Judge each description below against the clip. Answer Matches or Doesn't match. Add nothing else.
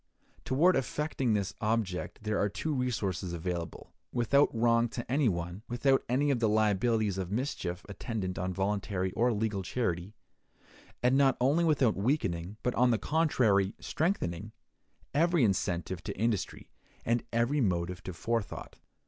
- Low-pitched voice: Matches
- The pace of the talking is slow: Doesn't match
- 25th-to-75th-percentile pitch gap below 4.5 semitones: Doesn't match